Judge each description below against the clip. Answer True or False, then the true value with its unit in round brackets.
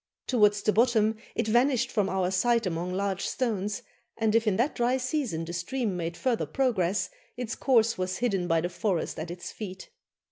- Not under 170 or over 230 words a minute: True (185 wpm)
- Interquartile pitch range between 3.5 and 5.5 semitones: True (4.7 semitones)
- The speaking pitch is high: True (210 Hz)